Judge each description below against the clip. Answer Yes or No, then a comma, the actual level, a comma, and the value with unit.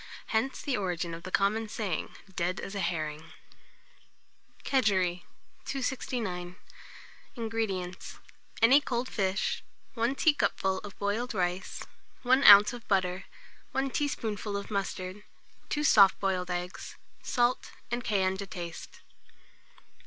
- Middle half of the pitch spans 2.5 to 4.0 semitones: No, average, 4.6 semitones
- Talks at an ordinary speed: No, slow, 115 wpm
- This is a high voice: Yes, high, 200 Hz